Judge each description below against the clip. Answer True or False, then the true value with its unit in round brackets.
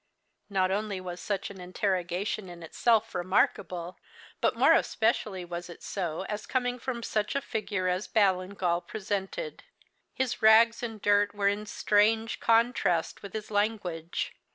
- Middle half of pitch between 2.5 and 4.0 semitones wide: True (3.2 semitones)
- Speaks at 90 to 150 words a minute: True (145 wpm)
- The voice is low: False (205 Hz)